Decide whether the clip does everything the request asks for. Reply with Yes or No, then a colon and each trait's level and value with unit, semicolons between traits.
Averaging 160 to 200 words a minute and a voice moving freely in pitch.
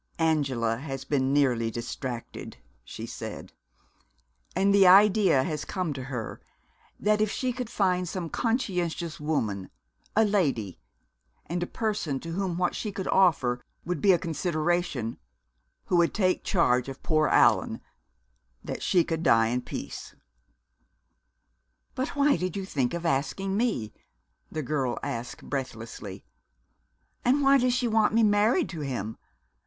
No: average, 145 wpm; wide, 7.0 semitones